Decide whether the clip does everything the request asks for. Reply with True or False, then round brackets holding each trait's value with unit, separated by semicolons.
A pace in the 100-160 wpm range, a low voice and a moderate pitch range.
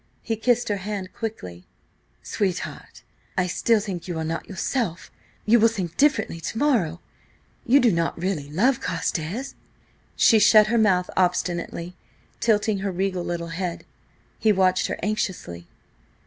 False (140 wpm; 190 Hz; 4.2 semitones)